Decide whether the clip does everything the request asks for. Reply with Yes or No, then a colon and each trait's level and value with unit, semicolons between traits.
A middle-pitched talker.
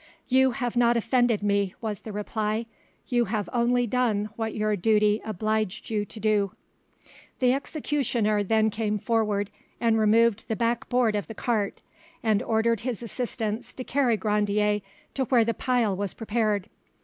No: high, 220 Hz